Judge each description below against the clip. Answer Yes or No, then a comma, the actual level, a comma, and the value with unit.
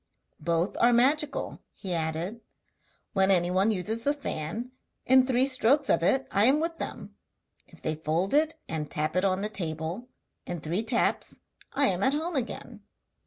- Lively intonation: Yes, wide, 7.4 semitones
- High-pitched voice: Yes, high, 205 Hz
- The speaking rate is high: No, average, 165 wpm